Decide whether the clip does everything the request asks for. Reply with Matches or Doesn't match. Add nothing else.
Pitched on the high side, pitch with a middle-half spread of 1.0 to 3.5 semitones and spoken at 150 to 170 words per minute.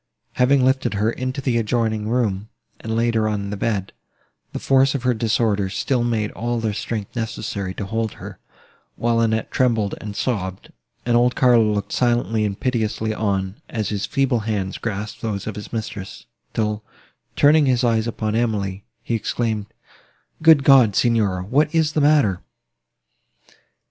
Doesn't match